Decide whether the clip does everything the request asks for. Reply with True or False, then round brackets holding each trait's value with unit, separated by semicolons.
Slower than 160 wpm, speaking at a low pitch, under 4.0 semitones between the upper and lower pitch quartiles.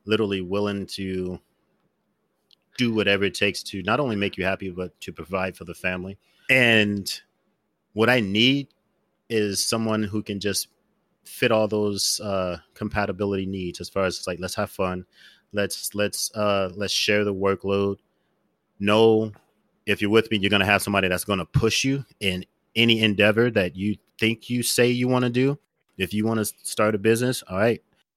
False (175 wpm; 105 Hz; 2.4 semitones)